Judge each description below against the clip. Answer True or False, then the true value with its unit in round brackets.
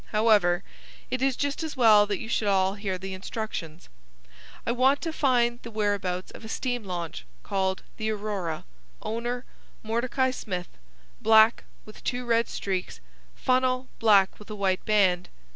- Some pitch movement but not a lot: True (4.1 semitones)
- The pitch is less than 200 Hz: False (215 Hz)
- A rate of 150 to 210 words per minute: True (155 wpm)